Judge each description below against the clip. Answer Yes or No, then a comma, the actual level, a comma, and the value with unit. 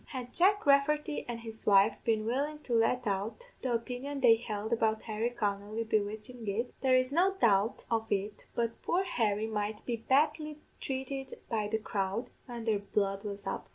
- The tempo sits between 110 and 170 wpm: No, average, 180 wpm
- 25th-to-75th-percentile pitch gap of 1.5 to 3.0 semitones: No, average, 3.8 semitones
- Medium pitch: No, high, 230 Hz